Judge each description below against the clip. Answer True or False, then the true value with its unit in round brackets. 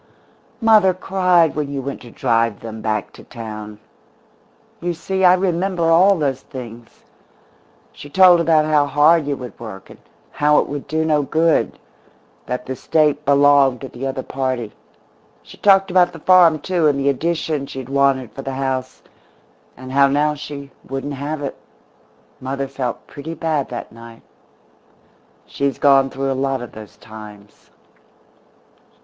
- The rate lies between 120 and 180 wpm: True (160 wpm)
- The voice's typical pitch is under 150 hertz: True (140 Hz)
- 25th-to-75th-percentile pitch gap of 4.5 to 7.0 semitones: False (3.7 semitones)